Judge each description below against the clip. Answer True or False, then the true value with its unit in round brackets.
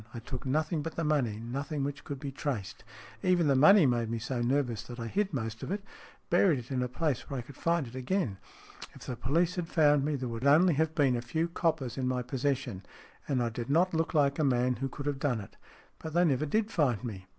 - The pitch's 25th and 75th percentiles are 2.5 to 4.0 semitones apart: False (4.5 semitones)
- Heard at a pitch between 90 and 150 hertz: True (140 Hz)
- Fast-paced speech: True (245 wpm)